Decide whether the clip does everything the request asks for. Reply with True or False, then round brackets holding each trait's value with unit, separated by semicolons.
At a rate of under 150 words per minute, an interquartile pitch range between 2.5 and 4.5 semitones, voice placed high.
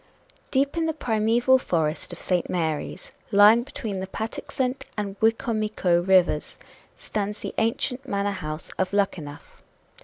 True (140 wpm; 4.2 semitones; 205 Hz)